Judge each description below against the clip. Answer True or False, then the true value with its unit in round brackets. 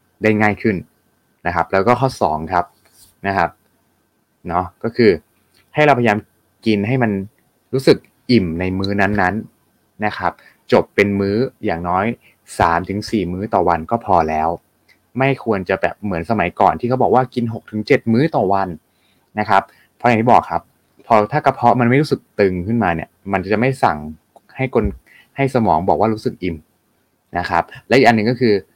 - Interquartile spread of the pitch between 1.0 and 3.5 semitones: False (4.5 semitones)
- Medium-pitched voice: False (105 Hz)